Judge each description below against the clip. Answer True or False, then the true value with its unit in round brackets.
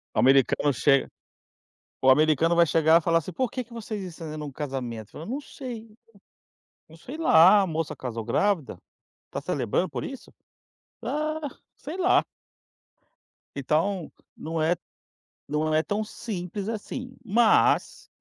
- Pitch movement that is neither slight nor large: False (6.5 semitones)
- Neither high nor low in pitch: True (170 Hz)